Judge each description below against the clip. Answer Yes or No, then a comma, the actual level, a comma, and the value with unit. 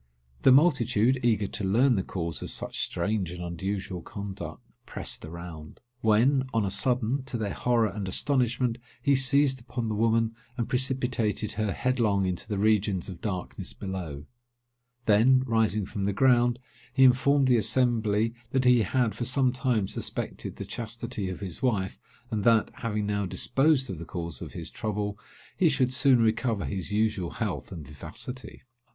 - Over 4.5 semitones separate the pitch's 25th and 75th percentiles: No, average, 4.2 semitones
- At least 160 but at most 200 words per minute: Yes, average, 165 wpm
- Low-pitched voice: Yes, low, 110 Hz